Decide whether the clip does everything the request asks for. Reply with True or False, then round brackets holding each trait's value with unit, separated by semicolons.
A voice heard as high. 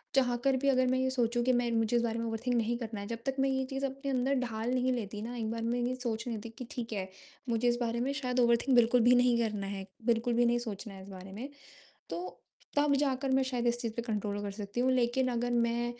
True (240 Hz)